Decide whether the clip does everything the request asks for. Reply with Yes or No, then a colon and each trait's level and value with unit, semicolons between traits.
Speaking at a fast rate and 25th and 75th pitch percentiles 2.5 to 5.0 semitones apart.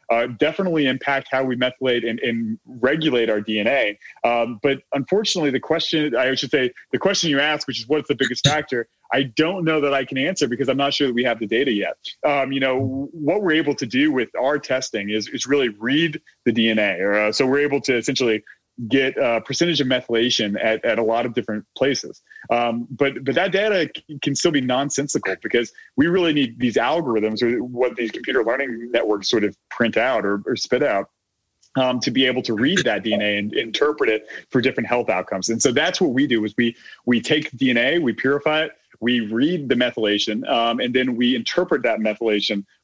Yes: fast, 210 wpm; average, 3.6 semitones